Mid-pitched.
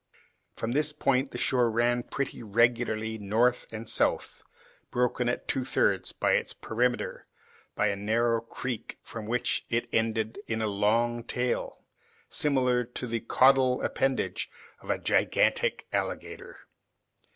No: low, 120 Hz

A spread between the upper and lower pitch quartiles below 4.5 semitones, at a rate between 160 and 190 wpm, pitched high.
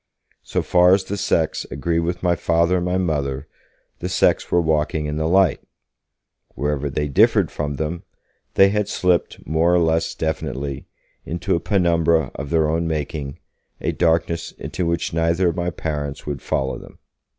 No: narrow, 2.6 semitones; average, 170 wpm; very low, 80 Hz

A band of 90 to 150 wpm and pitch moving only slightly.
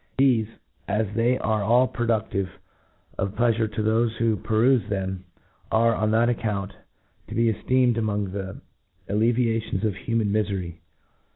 Yes: average, 145 wpm; narrow, 2.3 semitones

